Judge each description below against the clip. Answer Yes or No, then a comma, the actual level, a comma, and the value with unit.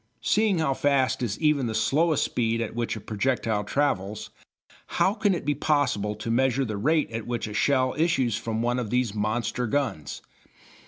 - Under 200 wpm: Yes, average, 180 wpm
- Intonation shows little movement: No, average, 4.5 semitones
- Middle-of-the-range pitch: No, low, 125 Hz